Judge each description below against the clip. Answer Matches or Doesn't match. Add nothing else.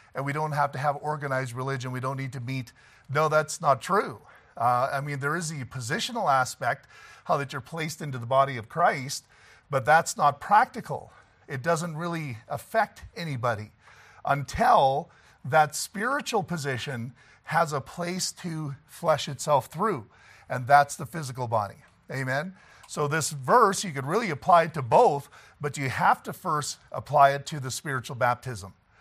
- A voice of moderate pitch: Matches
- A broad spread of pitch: Doesn't match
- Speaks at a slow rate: Doesn't match